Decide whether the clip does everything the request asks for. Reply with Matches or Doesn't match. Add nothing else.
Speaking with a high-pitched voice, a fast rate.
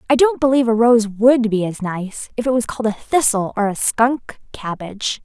Matches